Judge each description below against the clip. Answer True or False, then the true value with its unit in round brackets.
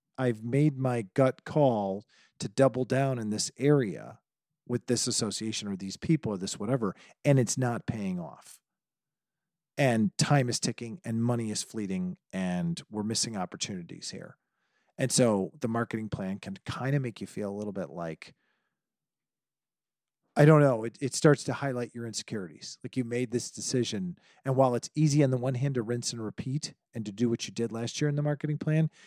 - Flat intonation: False (4.3 semitones)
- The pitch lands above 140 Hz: False (125 Hz)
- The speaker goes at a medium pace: True (190 wpm)